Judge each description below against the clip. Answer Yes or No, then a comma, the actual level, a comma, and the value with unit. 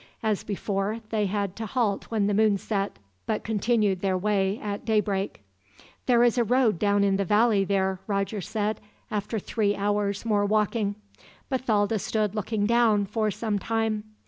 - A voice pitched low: No, high, 210 Hz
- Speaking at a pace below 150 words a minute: No, average, 165 wpm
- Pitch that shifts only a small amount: Yes, narrow, 1.7 semitones